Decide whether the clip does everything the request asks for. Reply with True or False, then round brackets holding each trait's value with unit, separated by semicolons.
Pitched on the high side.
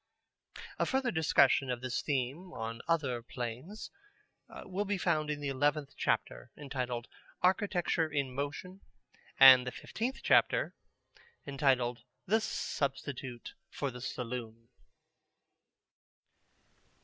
False (140 Hz)